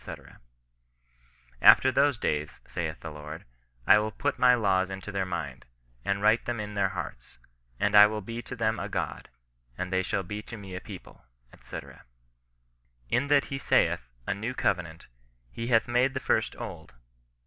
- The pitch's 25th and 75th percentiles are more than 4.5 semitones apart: Yes, average, 5.0 semitones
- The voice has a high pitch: No, low, 105 Hz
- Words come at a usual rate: Yes, average, 175 wpm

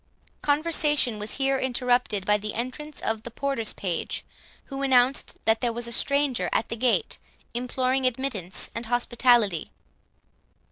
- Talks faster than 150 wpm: No, average, 140 wpm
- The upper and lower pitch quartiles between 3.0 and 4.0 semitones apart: Yes, average, 3.3 semitones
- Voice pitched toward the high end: Yes, high, 245 Hz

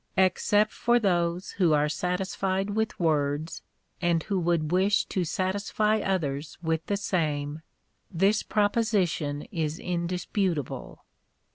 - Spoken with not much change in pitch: No, average, 3.8 semitones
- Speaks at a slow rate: Yes, slow, 120 wpm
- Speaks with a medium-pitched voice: Yes, medium, 180 Hz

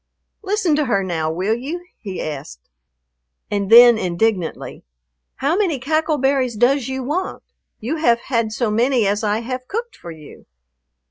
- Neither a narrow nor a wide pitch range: No, wide, 5.7 semitones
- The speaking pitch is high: Yes, high, 240 Hz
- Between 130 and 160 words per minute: Yes, average, 155 wpm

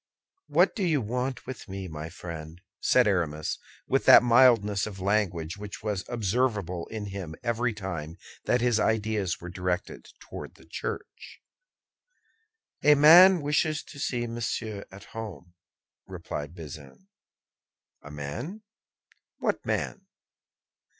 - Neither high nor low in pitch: No, low, 105 Hz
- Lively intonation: Yes, wide, 5.7 semitones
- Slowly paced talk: Yes, slow, 125 wpm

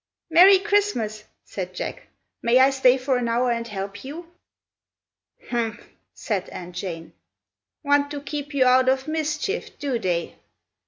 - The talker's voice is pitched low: No, very high, 255 Hz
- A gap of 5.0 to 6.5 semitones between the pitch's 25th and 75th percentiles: Yes, average, 5.3 semitones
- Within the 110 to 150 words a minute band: Yes, average, 145 wpm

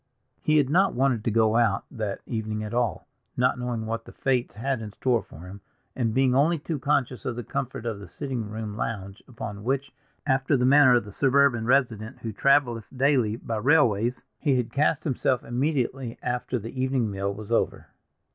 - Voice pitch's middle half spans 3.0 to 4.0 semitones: Yes, average, 3.5 semitones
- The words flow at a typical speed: Yes, average, 195 wpm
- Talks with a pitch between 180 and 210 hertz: No, low, 120 Hz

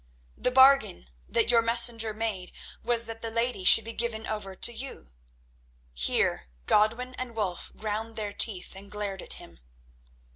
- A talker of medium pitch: No, high, 225 Hz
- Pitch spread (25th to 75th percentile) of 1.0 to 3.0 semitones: Yes, narrow, 2.5 semitones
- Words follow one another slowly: No, average, 155 wpm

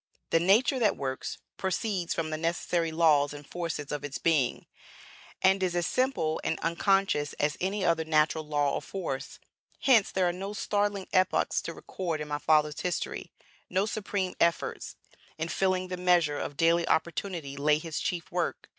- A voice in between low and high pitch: Yes, medium, 170 Hz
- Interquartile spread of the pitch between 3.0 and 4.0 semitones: Yes, average, 3.7 semitones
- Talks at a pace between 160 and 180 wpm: Yes, average, 170 wpm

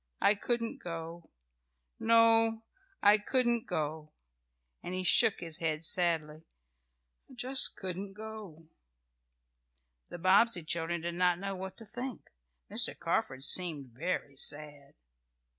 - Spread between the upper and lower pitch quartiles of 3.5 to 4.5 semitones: No, average, 5.3 semitones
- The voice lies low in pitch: No, medium, 180 Hz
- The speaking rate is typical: No, slow, 120 wpm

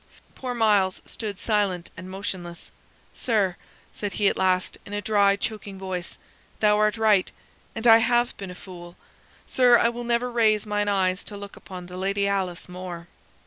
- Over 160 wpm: Yes, average, 175 wpm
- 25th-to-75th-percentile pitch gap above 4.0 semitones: No, average, 2.8 semitones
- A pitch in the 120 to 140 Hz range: No, high, 200 Hz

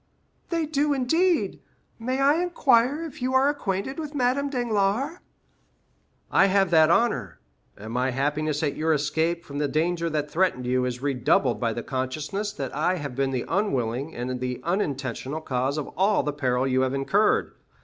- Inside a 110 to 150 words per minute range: No, average, 175 wpm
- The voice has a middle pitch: Yes, medium, 160 Hz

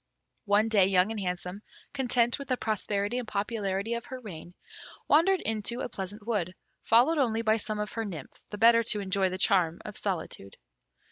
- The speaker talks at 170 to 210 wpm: Yes, average, 185 wpm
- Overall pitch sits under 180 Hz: No, high, 210 Hz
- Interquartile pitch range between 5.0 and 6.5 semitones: No, average, 3.3 semitones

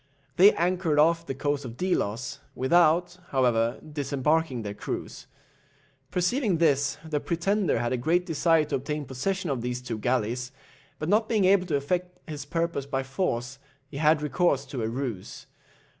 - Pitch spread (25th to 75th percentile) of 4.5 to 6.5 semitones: Yes, average, 5.2 semitones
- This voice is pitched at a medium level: Yes, medium, 150 Hz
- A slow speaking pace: No, average, 160 wpm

